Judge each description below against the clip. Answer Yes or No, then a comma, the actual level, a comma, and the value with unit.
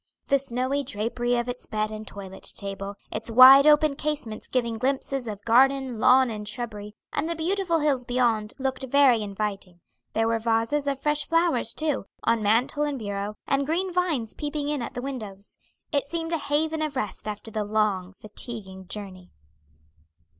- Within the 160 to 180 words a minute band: Yes, average, 170 wpm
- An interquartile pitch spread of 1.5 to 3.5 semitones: No, average, 5.1 semitones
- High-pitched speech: Yes, high, 245 Hz